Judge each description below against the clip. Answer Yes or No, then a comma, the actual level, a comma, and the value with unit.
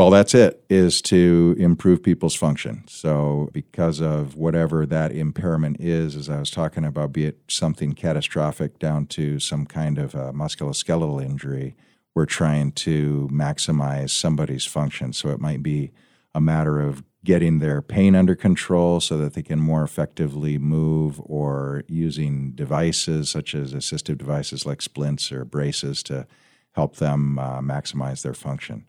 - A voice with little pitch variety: Yes, narrow, 2.0 semitones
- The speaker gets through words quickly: No, average, 155 wpm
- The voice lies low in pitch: Yes, very low, 75 Hz